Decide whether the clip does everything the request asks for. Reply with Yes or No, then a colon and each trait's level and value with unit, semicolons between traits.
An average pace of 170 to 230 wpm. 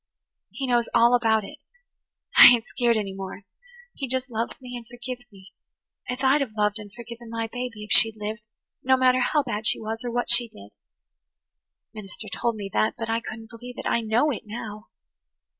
Yes: average, 200 wpm